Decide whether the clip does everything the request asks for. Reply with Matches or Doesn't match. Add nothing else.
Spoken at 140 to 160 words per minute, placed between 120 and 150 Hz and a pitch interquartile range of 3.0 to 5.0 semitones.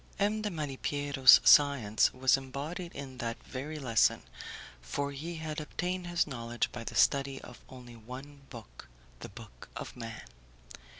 Matches